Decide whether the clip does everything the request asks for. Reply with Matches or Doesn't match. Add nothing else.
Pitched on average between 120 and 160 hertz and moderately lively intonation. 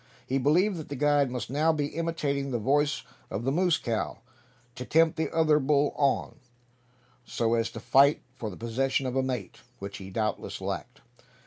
Matches